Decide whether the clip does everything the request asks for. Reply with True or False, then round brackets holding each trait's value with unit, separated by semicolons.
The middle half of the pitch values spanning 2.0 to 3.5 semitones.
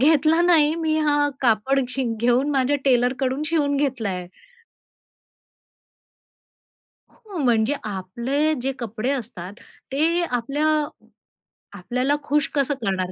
False (3.9 semitones)